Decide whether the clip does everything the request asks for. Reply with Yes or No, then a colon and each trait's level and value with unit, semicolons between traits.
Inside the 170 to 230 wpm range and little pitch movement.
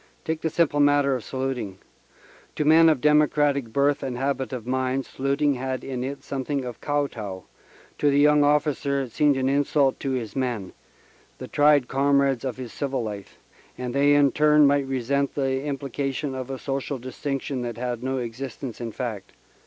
Yes: average, 180 wpm; narrow, 2.2 semitones